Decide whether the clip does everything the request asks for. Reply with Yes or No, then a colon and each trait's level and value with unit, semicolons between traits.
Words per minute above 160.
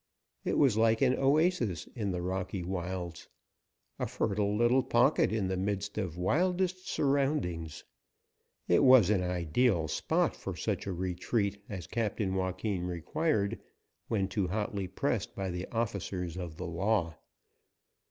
No: average, 140 wpm